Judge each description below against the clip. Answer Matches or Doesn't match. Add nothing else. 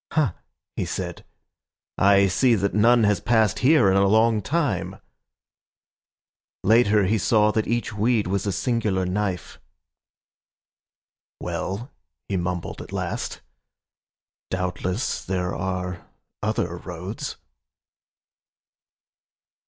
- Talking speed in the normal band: Doesn't match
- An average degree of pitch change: Matches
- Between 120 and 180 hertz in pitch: Doesn't match